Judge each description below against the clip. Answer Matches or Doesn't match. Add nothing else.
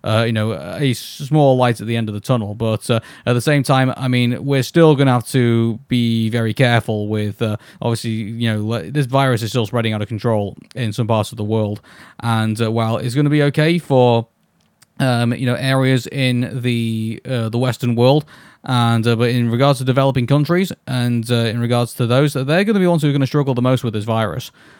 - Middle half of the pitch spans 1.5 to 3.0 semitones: Matches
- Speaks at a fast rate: Matches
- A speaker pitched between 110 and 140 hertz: Matches